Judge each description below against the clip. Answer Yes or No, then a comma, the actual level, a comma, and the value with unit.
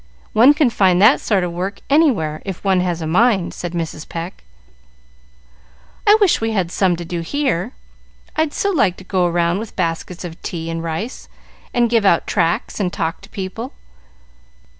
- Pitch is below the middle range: No, medium, 185 Hz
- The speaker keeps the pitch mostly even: No, average, 5.0 semitones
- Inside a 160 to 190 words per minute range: Yes, average, 180 wpm